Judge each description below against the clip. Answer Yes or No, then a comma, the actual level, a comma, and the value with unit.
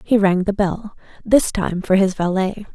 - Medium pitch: No, high, 195 Hz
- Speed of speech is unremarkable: Yes, average, 195 wpm